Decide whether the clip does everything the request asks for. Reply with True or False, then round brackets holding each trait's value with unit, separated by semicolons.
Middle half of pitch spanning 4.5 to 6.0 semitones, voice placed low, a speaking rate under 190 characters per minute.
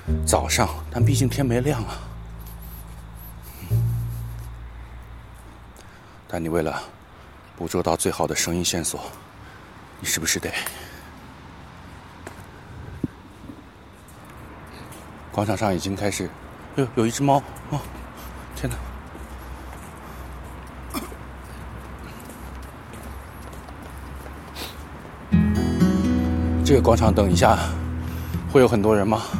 True (5.1 semitones; 85 Hz; 115 characters per minute)